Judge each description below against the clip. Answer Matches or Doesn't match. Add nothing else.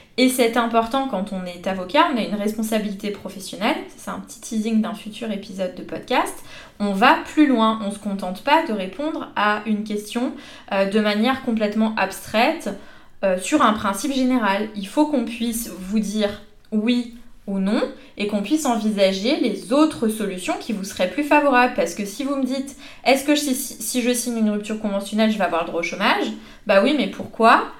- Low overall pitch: Doesn't match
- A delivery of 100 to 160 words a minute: Doesn't match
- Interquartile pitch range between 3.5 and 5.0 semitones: Matches